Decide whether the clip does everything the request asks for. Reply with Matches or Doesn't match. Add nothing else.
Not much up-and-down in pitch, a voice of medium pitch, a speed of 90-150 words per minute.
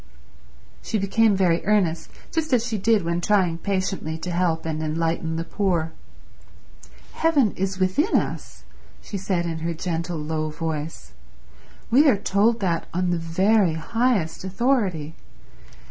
Doesn't match